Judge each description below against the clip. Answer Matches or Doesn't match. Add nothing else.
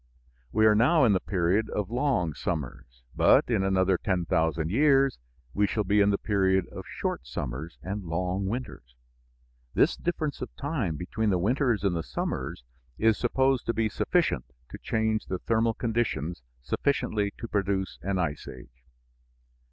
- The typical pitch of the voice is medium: Doesn't match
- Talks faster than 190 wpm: Doesn't match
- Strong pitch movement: Doesn't match